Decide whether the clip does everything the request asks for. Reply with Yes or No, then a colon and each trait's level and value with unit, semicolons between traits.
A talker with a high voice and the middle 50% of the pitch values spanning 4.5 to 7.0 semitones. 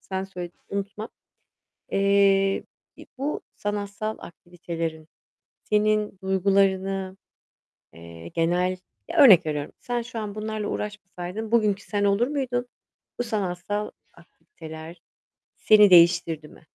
No: high, 195 Hz; average, 3.3 semitones